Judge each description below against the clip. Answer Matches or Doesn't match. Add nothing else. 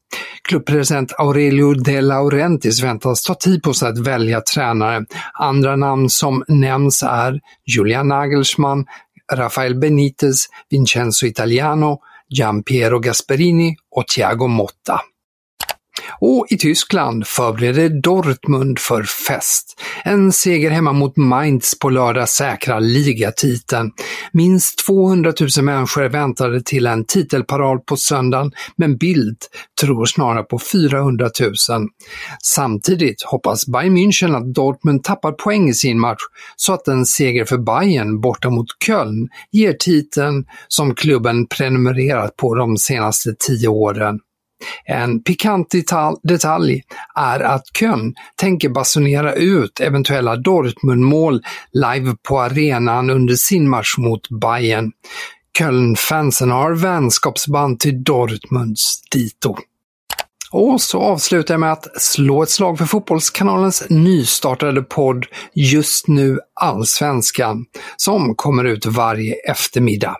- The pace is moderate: Doesn't match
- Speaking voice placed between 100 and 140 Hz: Matches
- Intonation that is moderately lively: Matches